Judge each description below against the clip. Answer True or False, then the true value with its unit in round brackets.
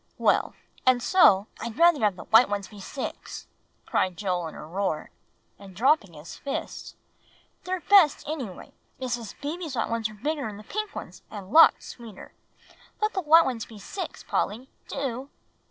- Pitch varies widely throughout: True (6.9 semitones)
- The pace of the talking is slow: False (170 wpm)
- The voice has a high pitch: True (235 Hz)